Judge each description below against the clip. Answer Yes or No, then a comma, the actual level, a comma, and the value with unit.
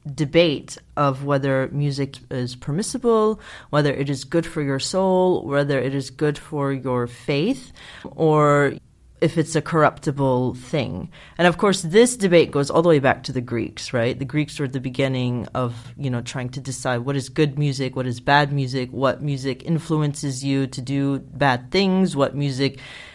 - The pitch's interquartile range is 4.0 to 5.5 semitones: No, average, 2.7 semitones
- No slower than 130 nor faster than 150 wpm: No, average, 180 wpm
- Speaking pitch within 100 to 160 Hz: Yes, medium, 140 Hz